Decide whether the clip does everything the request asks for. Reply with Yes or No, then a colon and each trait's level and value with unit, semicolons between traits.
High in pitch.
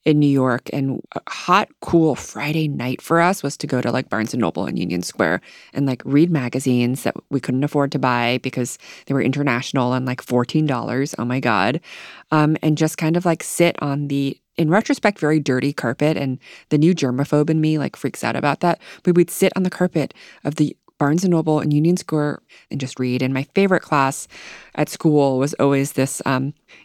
No: medium, 140 Hz